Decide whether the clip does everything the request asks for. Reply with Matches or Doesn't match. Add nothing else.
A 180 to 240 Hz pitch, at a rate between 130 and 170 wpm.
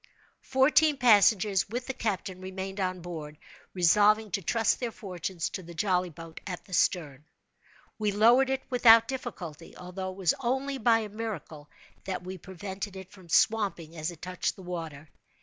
Matches